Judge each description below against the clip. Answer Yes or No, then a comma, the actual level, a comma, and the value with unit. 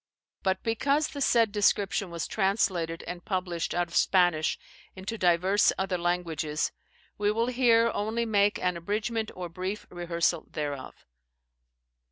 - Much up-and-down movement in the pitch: No, average, 3.8 semitones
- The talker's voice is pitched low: No, high, 190 Hz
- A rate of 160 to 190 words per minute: No, slow, 135 wpm